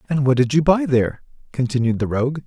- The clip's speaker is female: No, male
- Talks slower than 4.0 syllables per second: No, 6.5 syllables/s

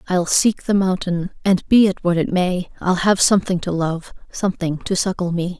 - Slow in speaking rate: No, fast, 205 wpm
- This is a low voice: No, medium, 180 Hz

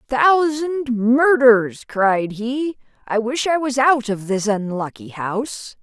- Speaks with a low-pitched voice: No, high, 240 Hz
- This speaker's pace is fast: No, slow, 135 wpm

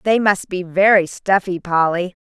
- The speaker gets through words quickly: No, average, 160 wpm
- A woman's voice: Yes, female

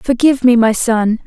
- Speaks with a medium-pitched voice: No, high, 240 Hz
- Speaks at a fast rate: No, average, 190 wpm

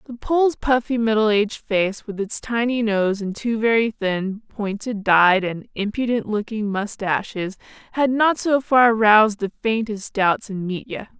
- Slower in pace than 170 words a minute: Yes, average, 160 wpm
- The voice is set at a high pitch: Yes, high, 215 Hz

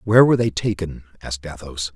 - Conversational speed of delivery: Yes, average, 185 wpm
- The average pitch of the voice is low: Yes, very low, 90 Hz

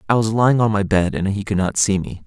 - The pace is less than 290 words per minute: No, fast, 315 wpm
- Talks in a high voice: No, low, 105 Hz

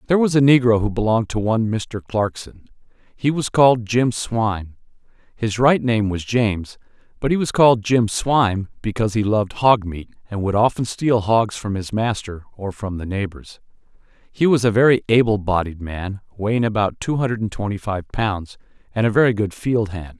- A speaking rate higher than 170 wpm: Yes, average, 190 wpm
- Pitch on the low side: Yes, low, 110 Hz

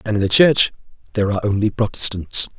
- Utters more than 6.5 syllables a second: Yes, 6.7 syllables/s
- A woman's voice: No, male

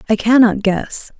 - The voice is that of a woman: Yes, female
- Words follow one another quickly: No, average, 150 wpm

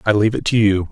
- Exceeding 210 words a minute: Yes, fast, 330 wpm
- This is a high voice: No, low, 105 Hz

